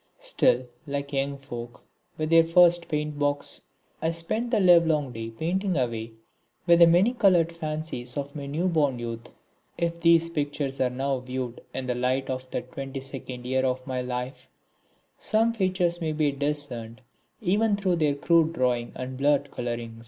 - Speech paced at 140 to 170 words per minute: Yes, average, 165 wpm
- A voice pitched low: No, medium, 145 Hz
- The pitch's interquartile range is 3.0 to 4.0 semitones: No, average, 4.7 semitones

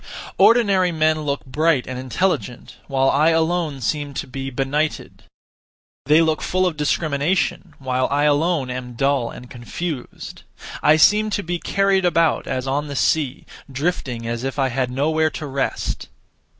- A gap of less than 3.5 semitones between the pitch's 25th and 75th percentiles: No, average, 3.8 semitones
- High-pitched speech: No, medium, 145 Hz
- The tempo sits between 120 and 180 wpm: Yes, average, 155 wpm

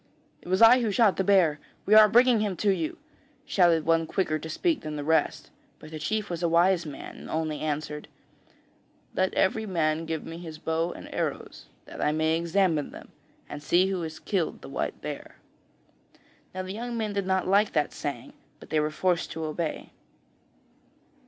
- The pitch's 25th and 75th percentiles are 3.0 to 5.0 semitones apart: Yes, average, 4.0 semitones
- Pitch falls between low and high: Yes, medium, 170 Hz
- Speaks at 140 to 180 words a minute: No, average, 190 wpm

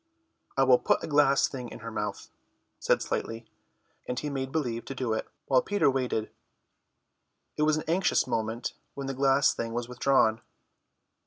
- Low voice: Yes, low, 130 Hz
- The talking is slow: No, average, 170 wpm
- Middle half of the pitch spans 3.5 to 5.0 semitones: No, average, 3.0 semitones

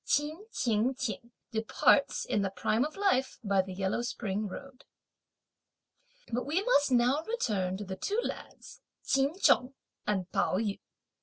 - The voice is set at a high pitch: Yes, high, 240 Hz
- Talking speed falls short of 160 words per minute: Yes, average, 150 wpm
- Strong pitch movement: Yes, wide, 6.1 semitones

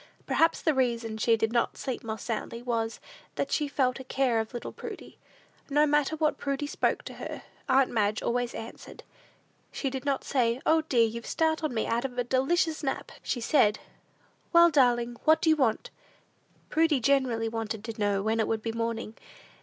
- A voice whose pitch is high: Yes, high, 245 Hz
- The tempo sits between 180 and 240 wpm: Yes, average, 185 wpm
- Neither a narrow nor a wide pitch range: Yes, average, 3.8 semitones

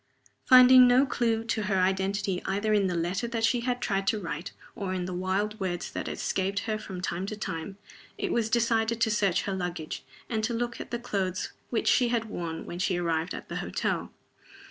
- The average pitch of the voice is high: Yes, high, 200 Hz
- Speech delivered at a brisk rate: Yes, fast, 210 wpm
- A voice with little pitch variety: No, average, 3.8 semitones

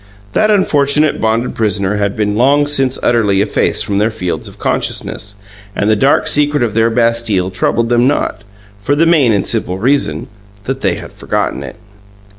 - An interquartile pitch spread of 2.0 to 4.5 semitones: No, average, 5.2 semitones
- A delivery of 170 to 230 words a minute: Yes, average, 175 wpm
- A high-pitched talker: No, low, 115 Hz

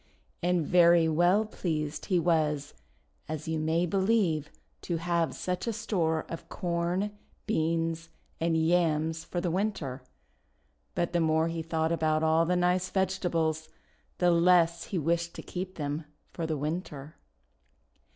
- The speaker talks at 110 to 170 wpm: Yes, average, 140 wpm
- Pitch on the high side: No, medium, 165 Hz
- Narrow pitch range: Yes, narrow, 1.9 semitones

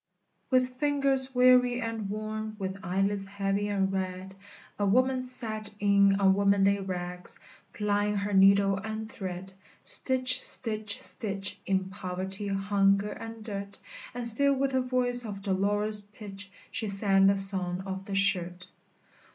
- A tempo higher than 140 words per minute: No, slow, 135 wpm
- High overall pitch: Yes, high, 200 Hz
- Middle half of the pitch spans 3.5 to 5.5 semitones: No, narrow, 2.6 semitones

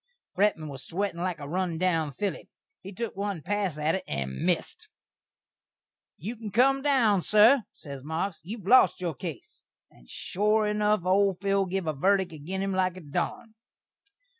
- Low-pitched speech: No, high, 190 Hz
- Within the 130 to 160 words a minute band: No, average, 170 wpm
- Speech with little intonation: No, average, 4.3 semitones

